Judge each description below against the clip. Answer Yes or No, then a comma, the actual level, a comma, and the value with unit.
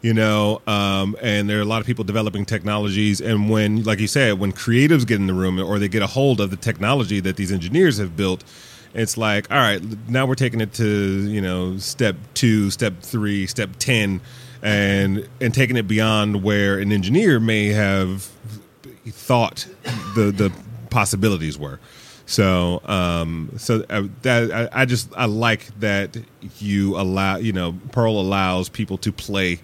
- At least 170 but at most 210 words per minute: Yes, average, 175 wpm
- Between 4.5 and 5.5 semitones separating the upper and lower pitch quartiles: No, average, 2.7 semitones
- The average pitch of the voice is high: No, low, 105 Hz